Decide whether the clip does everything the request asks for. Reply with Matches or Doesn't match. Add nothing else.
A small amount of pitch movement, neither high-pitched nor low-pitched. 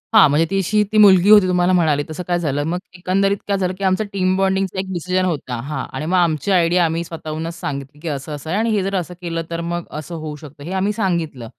Doesn't match